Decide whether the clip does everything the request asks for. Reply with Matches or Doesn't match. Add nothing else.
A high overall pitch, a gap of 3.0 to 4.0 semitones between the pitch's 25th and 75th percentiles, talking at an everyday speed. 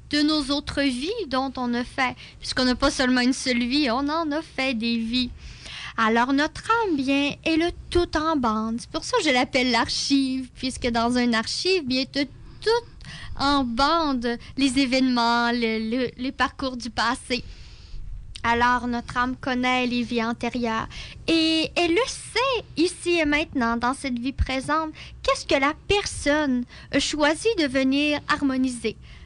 Matches